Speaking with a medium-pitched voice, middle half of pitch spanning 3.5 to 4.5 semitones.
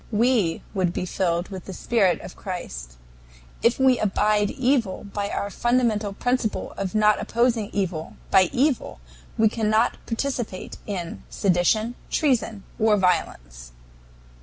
No: high, 210 Hz; average, 4.1 semitones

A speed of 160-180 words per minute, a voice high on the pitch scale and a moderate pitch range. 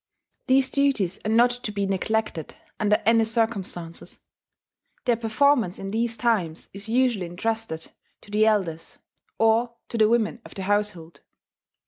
No: average, 140 wpm; high, 220 Hz; average, 3.2 semitones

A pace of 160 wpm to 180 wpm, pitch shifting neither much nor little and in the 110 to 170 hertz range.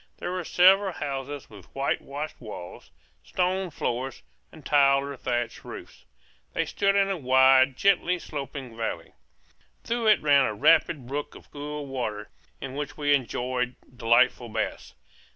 No: average, 145 wpm; average, 3.7 semitones; medium, 140 Hz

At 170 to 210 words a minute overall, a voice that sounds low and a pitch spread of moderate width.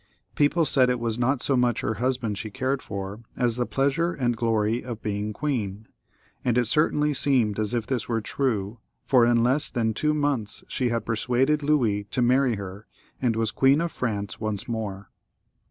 Yes: average, 185 wpm; low, 120 Hz; average, 3.7 semitones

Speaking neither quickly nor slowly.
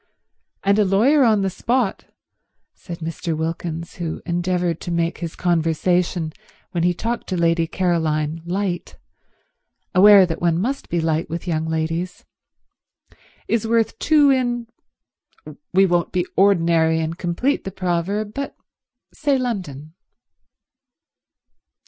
No: slow, 125 wpm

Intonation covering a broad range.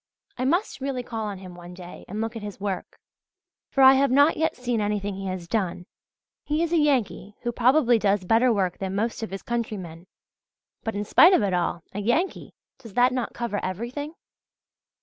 No: average, 4.8 semitones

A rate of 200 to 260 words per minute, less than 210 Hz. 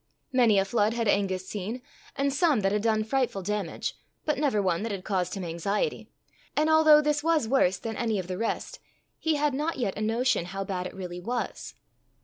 No: fast, 205 wpm; high, 220 Hz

